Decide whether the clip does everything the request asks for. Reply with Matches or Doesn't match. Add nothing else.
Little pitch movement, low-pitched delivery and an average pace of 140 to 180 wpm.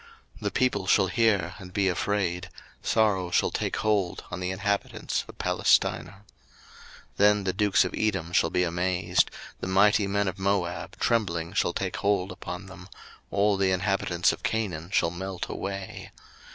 Matches